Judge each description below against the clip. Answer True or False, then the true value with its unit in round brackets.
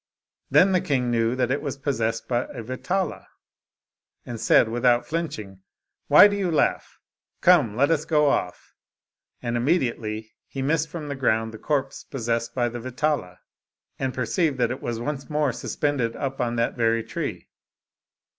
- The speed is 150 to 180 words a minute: True (165 wpm)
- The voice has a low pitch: True (130 Hz)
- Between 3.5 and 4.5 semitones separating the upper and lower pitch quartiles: True (4.2 semitones)